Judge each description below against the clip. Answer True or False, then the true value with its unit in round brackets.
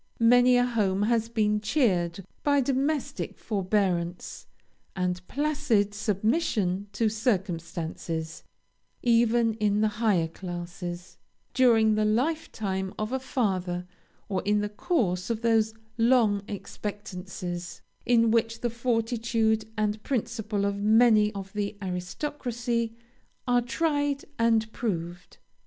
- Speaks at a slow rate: True (115 wpm)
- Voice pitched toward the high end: True (215 Hz)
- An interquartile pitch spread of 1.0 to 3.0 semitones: False (3.7 semitones)